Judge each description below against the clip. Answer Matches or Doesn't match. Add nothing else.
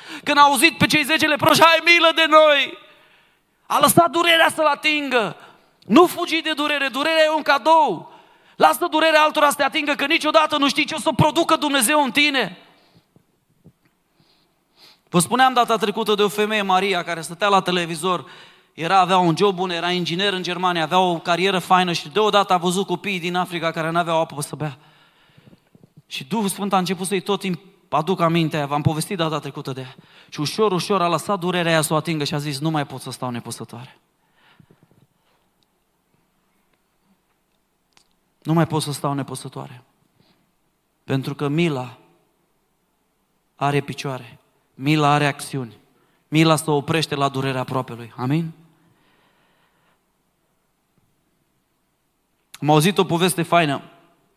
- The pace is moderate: Matches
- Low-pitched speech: Doesn't match